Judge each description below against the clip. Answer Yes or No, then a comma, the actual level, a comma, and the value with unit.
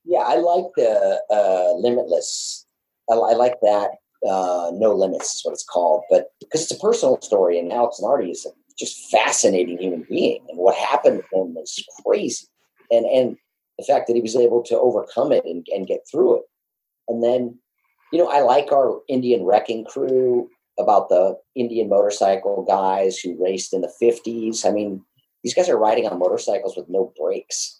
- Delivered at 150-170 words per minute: No, average, 185 wpm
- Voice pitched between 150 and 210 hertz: No, low, 120 Hz